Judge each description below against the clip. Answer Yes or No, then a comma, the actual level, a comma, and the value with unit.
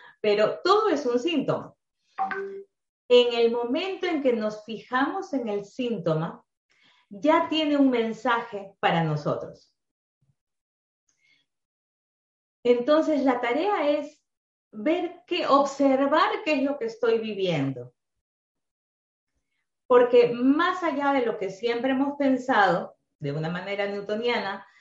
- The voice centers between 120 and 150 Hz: No, high, 240 Hz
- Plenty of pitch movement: Yes, wide, 6.4 semitones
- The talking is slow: Yes, slow, 115 wpm